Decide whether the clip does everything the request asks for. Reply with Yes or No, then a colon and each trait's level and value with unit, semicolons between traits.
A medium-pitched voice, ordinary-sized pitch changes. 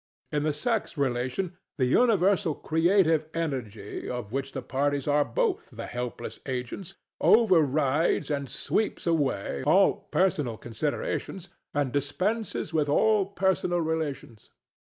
No: medium, 150 Hz; wide, 5.8 semitones